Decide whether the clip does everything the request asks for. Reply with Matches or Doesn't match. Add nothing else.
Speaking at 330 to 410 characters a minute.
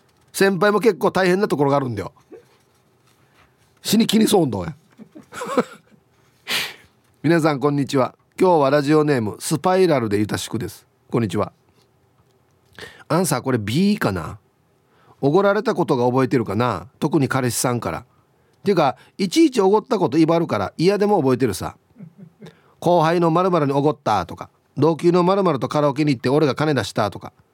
Matches